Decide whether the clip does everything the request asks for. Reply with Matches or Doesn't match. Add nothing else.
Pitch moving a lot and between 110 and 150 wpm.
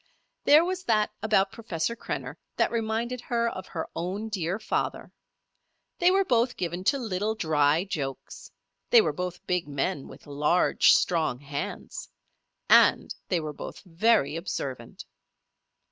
Matches